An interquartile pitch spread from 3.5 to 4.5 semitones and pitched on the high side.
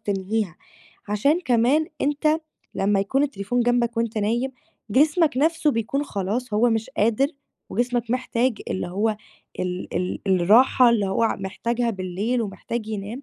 Yes: average, 4.0 semitones; high, 230 Hz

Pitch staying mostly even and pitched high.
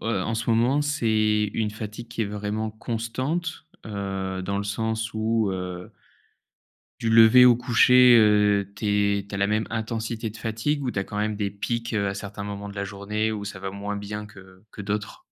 No: narrow, 2.0 semitones; low, 105 Hz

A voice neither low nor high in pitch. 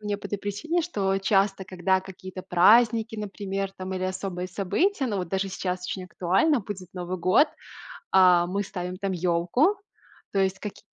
No: high, 195 Hz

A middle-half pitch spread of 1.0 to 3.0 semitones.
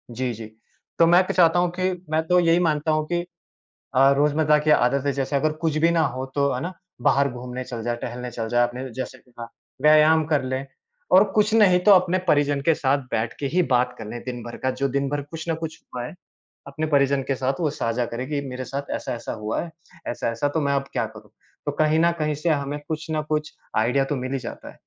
No: average, 3.8 semitones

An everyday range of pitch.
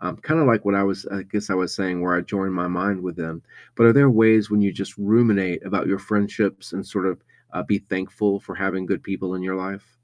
No: narrow, 2.0 semitones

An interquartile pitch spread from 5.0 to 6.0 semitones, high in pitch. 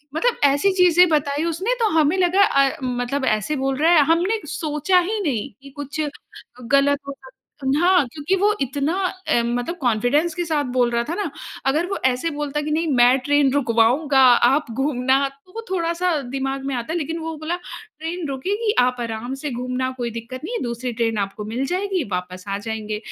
Yes: average, 5.3 semitones; very high, 280 Hz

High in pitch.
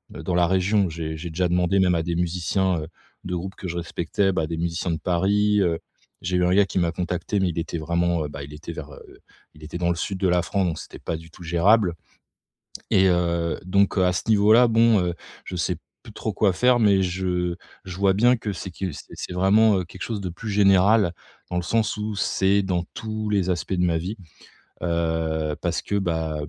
No: very low, 90 Hz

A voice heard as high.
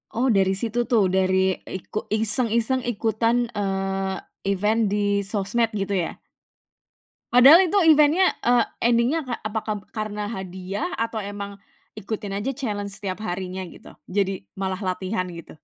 Yes: high, 210 Hz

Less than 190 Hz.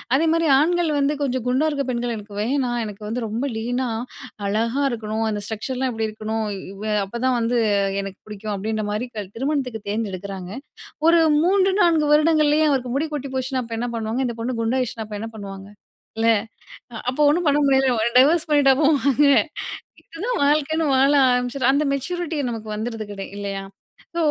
No: very high, 250 Hz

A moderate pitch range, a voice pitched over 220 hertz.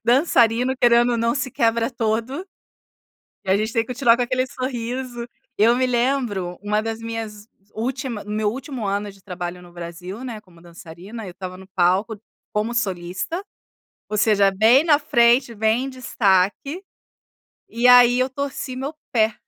Yes: average, 3.6 semitones; high, 230 Hz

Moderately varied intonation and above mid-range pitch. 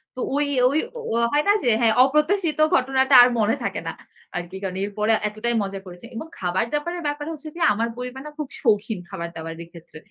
No: wide, 7.0 semitones; high, 235 Hz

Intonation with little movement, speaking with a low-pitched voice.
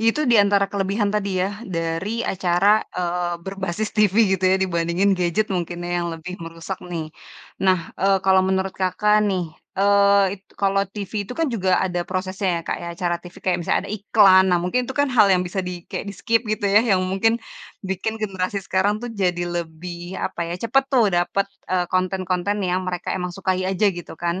No: narrow, 2.2 semitones; high, 190 Hz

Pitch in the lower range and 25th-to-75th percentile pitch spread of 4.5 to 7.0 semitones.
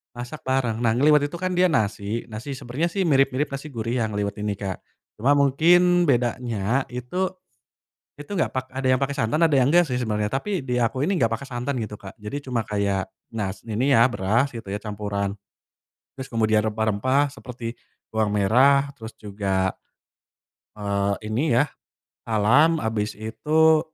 Yes: low, 120 Hz; average, 4.8 semitones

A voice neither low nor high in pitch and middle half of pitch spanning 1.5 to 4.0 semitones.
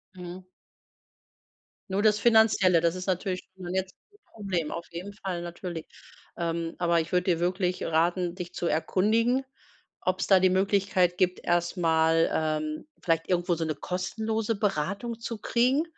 Yes: medium, 180 Hz; average, 2.9 semitones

